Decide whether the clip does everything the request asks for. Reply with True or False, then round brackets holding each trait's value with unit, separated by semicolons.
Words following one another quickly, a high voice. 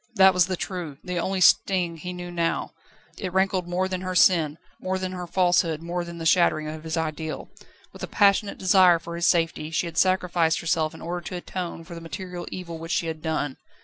False (220 wpm; 175 Hz)